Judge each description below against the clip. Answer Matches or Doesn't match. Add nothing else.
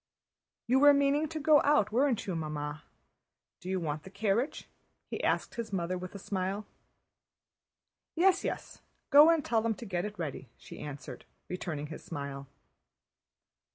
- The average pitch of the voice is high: Matches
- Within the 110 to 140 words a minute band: Doesn't match